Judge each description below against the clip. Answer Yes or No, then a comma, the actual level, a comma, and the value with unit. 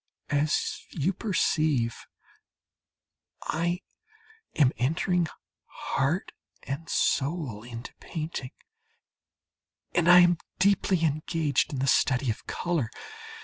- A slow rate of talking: Yes, slow, 95 wpm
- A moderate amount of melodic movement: Yes, average, 4.4 semitones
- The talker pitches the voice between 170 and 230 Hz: No, medium, 155 Hz